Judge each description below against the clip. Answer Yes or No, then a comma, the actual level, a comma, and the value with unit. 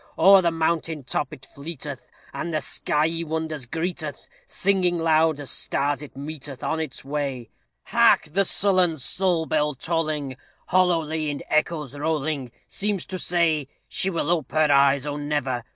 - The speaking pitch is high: No, medium, 155 Hz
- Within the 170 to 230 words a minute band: No, average, 150 wpm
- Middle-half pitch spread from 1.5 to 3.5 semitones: Yes, average, 2.7 semitones